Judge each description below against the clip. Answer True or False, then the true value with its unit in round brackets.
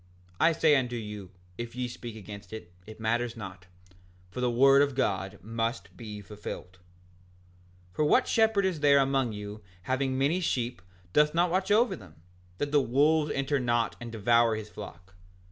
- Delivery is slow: False (175 wpm)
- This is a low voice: True (120 Hz)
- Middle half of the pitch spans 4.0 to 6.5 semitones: True (5.0 semitones)